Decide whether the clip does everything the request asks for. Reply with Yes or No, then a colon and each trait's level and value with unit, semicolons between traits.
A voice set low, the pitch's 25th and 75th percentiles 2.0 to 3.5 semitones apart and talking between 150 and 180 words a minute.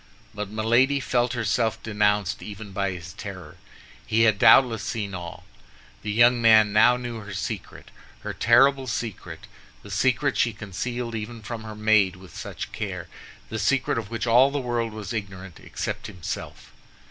Yes: low, 110 Hz; narrow, 2.6 semitones; average, 160 wpm